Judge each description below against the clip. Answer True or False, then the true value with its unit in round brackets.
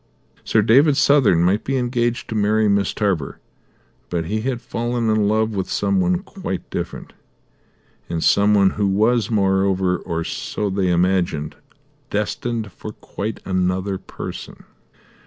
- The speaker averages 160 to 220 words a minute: False (140 wpm)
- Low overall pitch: True (105 Hz)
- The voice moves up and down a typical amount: True (3.8 semitones)